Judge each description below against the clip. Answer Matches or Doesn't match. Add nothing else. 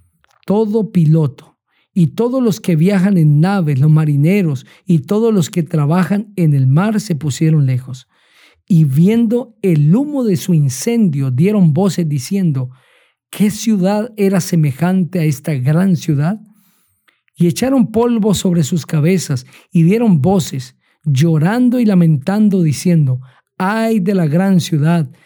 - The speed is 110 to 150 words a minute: Matches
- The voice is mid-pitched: Matches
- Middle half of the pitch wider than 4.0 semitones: Matches